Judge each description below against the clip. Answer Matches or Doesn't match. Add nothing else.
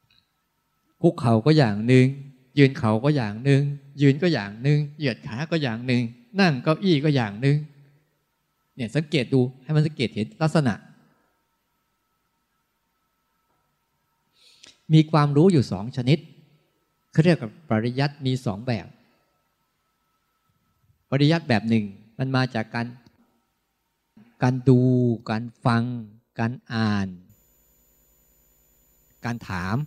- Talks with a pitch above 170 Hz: Doesn't match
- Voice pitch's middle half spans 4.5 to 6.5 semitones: Matches